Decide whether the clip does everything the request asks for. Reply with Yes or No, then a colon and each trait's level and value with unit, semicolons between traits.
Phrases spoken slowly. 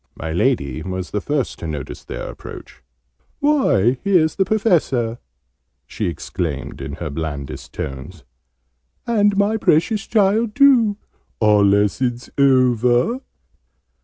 Yes: slow, 115 wpm